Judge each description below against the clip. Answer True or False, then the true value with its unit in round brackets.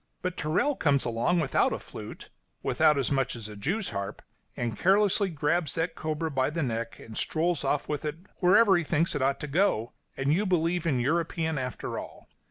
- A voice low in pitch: False (155 Hz)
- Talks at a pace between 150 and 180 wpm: False (200 wpm)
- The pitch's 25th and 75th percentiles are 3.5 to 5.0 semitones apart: True (4.6 semitones)